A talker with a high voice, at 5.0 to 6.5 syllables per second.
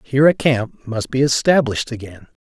No: low, 125 Hz; 5.5 syllables/s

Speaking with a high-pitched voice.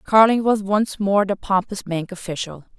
Yes: high, 195 Hz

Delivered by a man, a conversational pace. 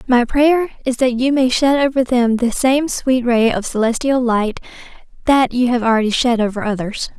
No: female; average, 190 wpm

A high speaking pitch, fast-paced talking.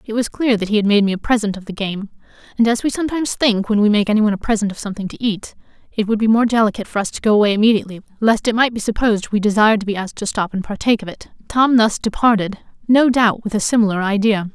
Yes: high, 215 Hz; fast, 265 wpm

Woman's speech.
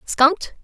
Yes: female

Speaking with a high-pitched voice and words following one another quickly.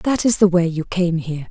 No: medium, 180 Hz; fast, 280 wpm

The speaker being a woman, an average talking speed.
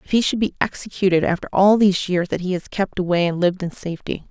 No: female; fast, 250 wpm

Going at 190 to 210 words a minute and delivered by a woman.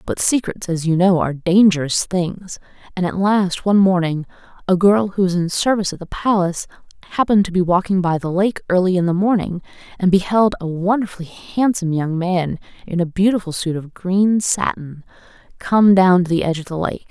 Yes: average, 195 wpm; female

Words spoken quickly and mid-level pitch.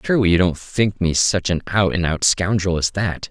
No: fast, 235 wpm; very low, 90 Hz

